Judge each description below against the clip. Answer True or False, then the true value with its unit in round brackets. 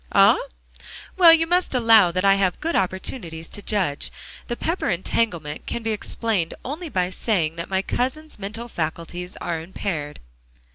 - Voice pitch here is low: False (195 Hz)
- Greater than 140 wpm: True (155 wpm)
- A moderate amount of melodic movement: False (5.7 semitones)